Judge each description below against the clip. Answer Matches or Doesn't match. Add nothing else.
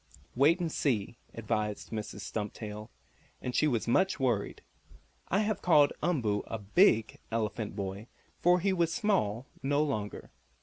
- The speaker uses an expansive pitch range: Matches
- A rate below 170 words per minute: Matches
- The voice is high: Doesn't match